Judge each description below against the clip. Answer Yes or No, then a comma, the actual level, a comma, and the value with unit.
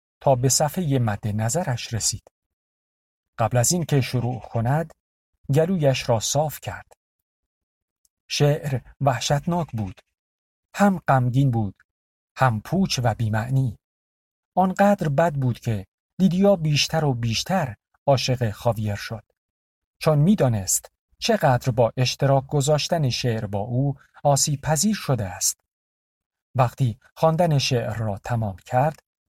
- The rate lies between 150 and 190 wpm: No, average, 115 wpm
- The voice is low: Yes, low, 130 Hz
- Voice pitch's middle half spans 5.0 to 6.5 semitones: Yes, wide, 5.4 semitones